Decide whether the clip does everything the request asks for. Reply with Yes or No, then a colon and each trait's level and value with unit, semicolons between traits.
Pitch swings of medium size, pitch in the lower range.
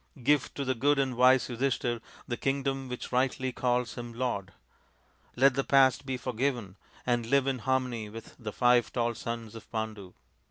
No: narrow, 2.2 semitones; low, 125 Hz